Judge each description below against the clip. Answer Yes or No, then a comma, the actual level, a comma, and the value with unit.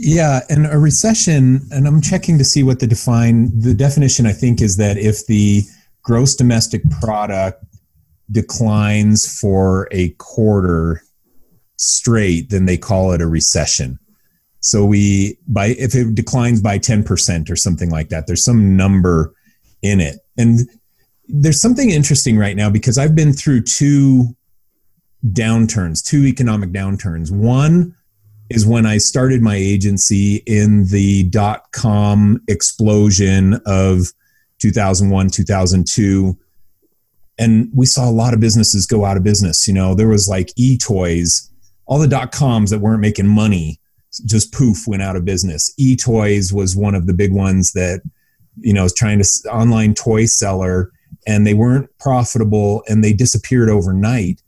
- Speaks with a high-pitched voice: No, low, 105 Hz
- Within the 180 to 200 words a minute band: No, average, 150 wpm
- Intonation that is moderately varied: Yes, average, 3.8 semitones